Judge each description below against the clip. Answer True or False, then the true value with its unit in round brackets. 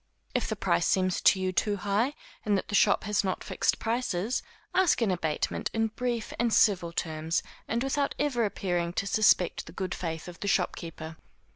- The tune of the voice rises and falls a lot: False (4.4 semitones)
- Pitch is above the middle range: True (195 Hz)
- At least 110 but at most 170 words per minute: False (185 wpm)